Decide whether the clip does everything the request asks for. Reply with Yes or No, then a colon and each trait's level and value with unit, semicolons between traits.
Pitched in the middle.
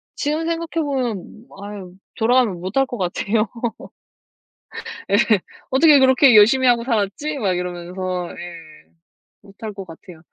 No: high, 215 Hz